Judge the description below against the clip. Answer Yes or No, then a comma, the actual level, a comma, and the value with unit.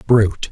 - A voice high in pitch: No, low, 110 Hz